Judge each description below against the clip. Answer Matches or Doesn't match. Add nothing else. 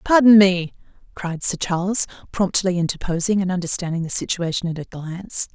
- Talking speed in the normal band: Matches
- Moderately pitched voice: Matches